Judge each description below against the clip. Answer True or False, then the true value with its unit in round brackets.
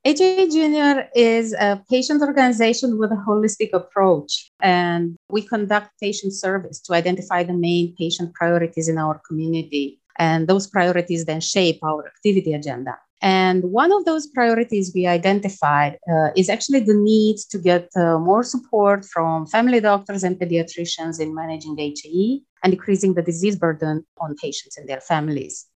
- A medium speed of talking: True (160 wpm)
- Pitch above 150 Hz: True (185 Hz)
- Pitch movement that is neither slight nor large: True (4.4 semitones)